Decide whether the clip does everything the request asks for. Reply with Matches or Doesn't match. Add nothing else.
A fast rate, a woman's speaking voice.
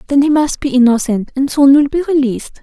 Matches